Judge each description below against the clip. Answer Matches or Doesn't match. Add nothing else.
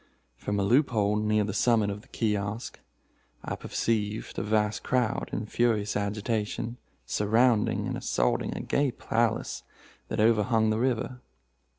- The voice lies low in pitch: Matches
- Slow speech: Doesn't match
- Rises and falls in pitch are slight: Matches